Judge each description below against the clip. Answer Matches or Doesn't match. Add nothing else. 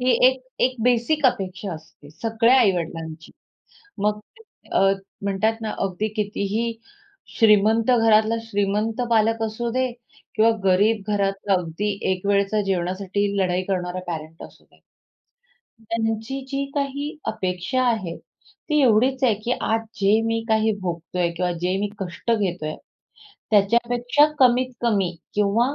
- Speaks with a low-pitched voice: Doesn't match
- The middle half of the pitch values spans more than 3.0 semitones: Matches